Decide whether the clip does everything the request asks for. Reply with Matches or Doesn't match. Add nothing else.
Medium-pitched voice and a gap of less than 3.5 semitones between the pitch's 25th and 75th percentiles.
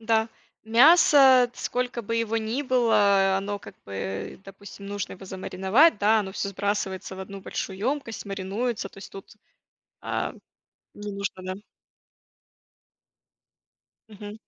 Doesn't match